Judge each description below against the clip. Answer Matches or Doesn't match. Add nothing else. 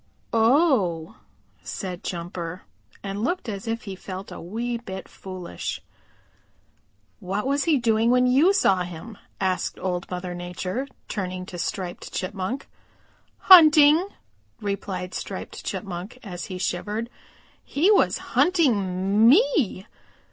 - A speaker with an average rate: Doesn't match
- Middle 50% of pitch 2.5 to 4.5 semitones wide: Doesn't match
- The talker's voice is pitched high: Matches